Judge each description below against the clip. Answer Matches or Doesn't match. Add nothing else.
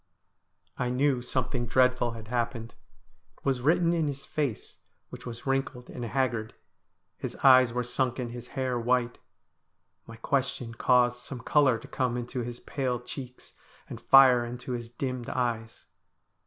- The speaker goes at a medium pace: Matches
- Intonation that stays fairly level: Matches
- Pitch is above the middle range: Doesn't match